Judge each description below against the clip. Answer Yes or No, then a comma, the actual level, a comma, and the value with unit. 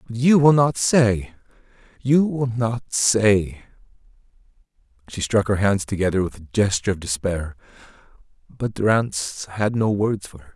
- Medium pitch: No, low, 105 Hz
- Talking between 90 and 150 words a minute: Yes, average, 140 wpm